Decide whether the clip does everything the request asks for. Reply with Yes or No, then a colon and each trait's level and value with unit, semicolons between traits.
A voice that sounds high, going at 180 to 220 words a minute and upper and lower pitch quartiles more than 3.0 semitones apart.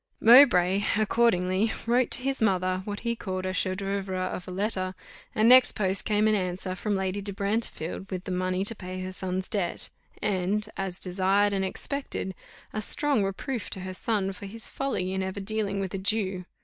No: high, 195 Hz; average, 190 wpm; narrow, 2.5 semitones